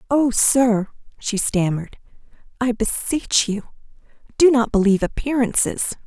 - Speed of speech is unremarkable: No, slow, 110 wpm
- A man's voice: No, female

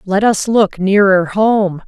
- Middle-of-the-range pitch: No, high, 200 Hz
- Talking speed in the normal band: Yes, average, 160 wpm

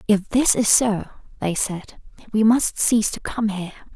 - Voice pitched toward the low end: No, high, 210 Hz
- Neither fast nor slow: Yes, average, 180 wpm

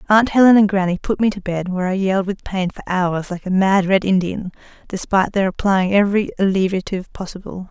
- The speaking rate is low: No, average, 200 wpm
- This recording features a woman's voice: Yes, female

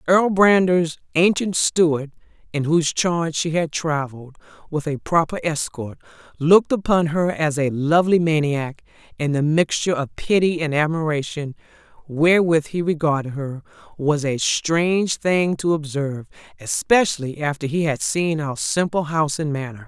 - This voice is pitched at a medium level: Yes, medium, 160 Hz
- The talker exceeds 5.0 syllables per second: No, 4.9 syllables/s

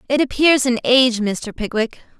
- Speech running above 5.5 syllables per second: No, 5.0 syllables/s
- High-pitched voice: Yes, high, 245 Hz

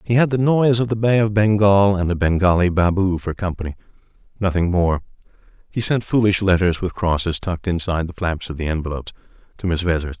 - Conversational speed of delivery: Yes, average, 195 wpm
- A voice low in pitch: Yes, very low, 95 Hz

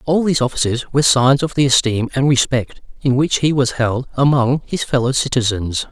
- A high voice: No, low, 130 Hz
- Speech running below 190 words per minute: No, average, 195 wpm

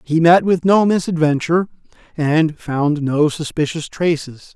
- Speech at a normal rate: No, slow, 130 wpm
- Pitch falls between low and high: Yes, medium, 160 Hz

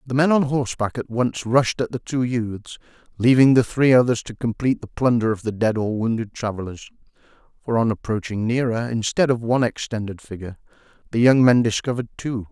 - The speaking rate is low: No, average, 185 wpm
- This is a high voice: No, low, 120 Hz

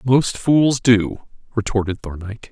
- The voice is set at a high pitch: No, low, 115 Hz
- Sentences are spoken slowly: Yes, slow, 120 wpm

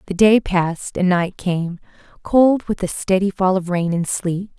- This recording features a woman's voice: Yes, female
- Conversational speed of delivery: Yes, average, 195 wpm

